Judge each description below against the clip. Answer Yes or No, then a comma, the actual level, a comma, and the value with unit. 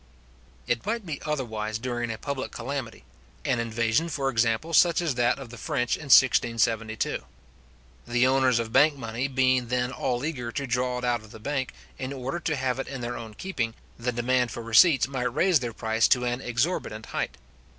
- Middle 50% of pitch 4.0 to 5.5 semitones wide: No, average, 2.7 semitones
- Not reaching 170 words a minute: No, average, 190 wpm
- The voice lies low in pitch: Yes, low, 125 Hz